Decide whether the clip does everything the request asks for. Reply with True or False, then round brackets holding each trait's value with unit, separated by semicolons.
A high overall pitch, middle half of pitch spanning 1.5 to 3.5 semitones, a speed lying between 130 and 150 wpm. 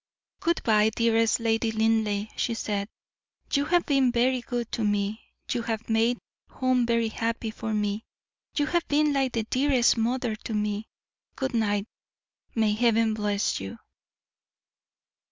True (225 Hz; 2.4 semitones; 145 wpm)